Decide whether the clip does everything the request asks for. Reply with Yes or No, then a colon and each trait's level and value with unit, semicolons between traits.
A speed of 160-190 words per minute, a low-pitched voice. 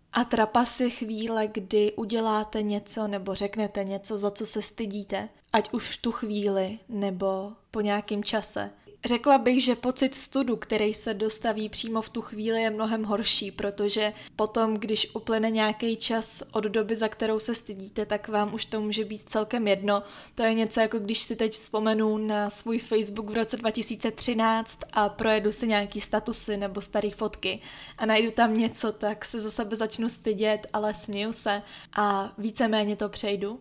No: fast, 170 wpm; high, 220 Hz